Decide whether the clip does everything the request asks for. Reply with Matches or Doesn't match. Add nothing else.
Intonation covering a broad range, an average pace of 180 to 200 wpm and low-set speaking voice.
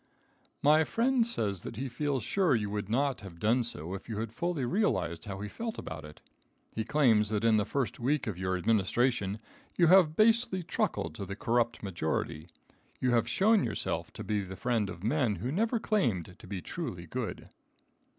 Matches